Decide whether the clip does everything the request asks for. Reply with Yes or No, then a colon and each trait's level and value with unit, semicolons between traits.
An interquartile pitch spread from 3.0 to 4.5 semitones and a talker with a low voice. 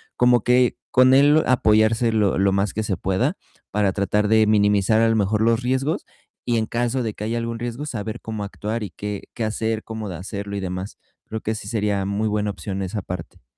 No: narrow, 2.4 semitones; low, 110 Hz